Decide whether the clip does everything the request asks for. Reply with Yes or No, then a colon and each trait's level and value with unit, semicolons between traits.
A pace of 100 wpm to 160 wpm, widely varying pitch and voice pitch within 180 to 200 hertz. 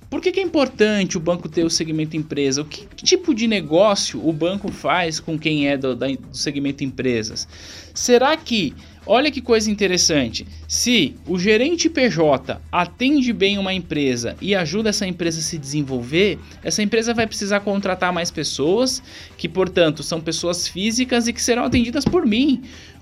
No: average, 170 wpm; wide, 7.2 semitones; medium, 185 Hz